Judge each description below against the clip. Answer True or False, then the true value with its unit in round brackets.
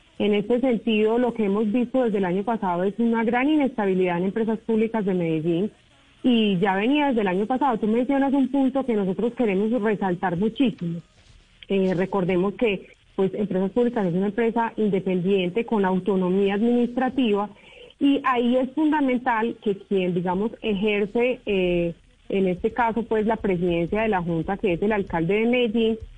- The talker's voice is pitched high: True (215 Hz)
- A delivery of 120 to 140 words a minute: False (165 wpm)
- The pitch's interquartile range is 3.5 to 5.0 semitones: True (3.9 semitones)